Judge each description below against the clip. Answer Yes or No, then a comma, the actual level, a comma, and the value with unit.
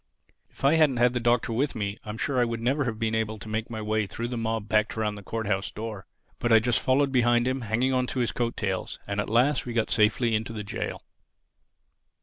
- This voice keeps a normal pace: No, fast, 250 wpm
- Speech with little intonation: Yes, narrow, 2.3 semitones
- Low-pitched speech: Yes, low, 115 Hz